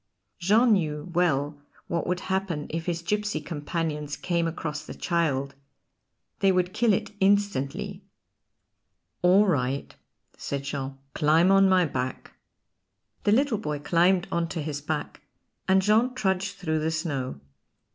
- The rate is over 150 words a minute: No, slow, 135 wpm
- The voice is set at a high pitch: No, medium, 170 Hz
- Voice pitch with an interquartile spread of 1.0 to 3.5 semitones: No, average, 4.4 semitones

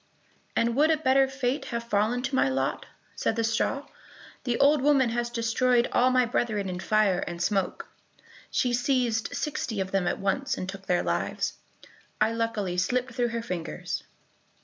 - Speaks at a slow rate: No, average, 170 wpm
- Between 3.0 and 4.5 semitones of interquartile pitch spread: Yes, average, 4.2 semitones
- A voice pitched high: Yes, high, 235 Hz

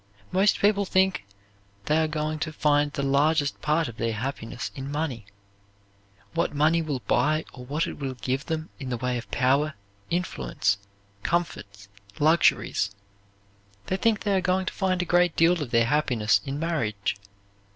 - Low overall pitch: No, medium, 150 Hz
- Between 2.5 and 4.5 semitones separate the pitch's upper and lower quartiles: No, average, 4.9 semitones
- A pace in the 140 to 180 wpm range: Yes, average, 165 wpm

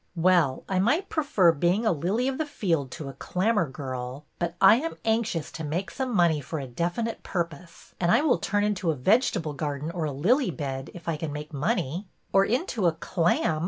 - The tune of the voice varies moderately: No, wide, 6.0 semitones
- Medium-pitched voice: Yes, medium, 175 Hz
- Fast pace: Yes, fast, 215 wpm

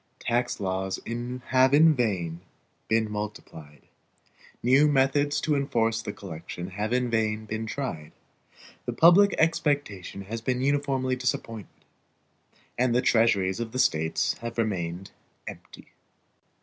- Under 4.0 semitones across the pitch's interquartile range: No, average, 5.0 semitones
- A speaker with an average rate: No, slow, 125 wpm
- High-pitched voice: No, low, 115 Hz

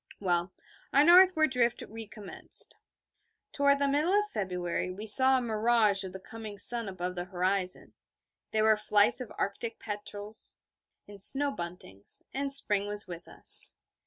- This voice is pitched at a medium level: No, high, 210 Hz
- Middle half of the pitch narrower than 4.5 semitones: No, average, 5.2 semitones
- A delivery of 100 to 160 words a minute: Yes, average, 150 wpm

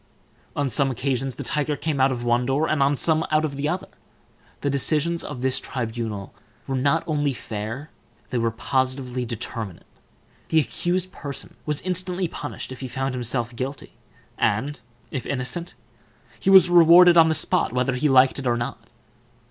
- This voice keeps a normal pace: Yes, average, 170 wpm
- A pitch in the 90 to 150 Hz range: Yes, low, 135 Hz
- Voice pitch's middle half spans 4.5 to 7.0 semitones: No, average, 3.7 semitones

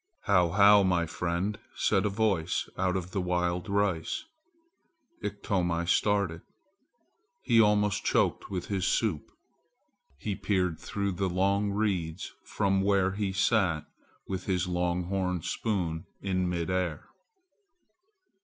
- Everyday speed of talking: No, slow, 125 wpm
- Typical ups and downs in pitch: No, narrow, 2.3 semitones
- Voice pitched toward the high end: No, very low, 95 Hz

